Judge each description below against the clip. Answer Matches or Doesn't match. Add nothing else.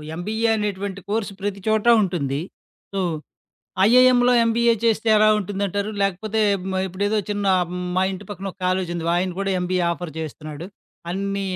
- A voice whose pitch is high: Matches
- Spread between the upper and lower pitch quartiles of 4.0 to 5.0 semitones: Doesn't match